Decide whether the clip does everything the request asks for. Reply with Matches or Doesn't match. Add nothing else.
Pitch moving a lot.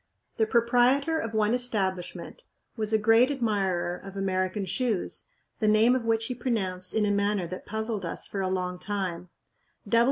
Doesn't match